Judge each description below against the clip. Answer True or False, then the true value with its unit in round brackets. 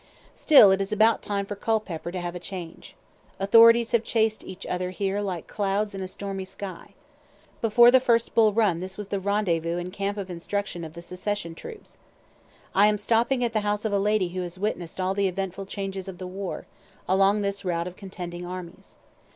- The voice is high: True (195 Hz)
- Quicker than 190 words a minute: True (200 wpm)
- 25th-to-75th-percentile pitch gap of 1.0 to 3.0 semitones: True (2.5 semitones)